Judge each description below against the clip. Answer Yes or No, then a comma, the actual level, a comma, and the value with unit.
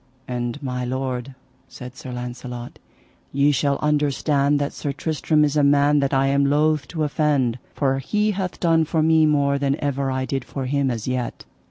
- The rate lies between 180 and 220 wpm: Yes, average, 185 wpm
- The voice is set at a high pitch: No, medium, 140 Hz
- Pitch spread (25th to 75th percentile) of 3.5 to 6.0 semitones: No, narrow, 2.4 semitones